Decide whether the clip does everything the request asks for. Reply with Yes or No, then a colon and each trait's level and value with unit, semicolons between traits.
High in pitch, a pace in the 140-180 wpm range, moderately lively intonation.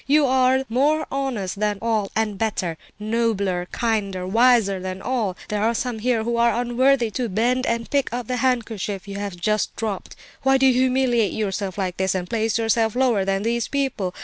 No: high, 225 Hz; average, 190 wpm; average, 3.9 semitones